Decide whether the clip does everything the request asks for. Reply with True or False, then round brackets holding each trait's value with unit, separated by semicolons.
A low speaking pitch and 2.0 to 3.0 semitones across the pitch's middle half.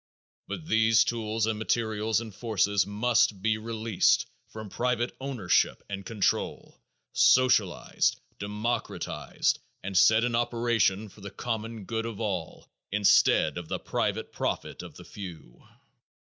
True (110 Hz; 2.4 semitones)